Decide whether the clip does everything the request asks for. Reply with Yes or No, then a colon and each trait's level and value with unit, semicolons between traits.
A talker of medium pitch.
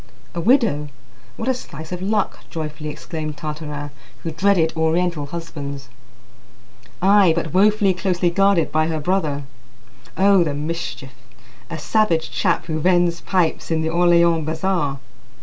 Yes: medium, 165 Hz